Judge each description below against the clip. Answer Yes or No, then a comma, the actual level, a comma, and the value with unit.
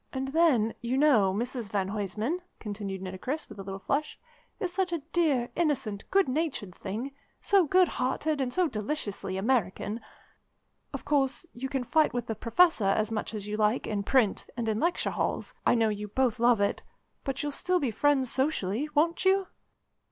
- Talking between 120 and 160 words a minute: No, average, 180 wpm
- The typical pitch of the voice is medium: No, high, 245 Hz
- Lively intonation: Yes, wide, 6.3 semitones